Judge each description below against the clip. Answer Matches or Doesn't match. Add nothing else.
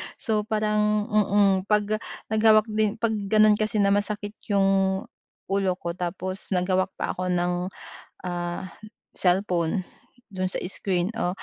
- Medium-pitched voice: Doesn't match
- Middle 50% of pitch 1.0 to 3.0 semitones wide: Matches